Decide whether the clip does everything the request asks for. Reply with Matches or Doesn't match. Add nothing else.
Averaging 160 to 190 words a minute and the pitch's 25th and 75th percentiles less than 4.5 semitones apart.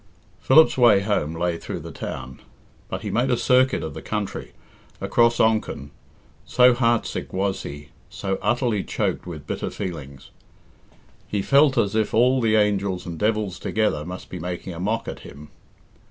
Doesn't match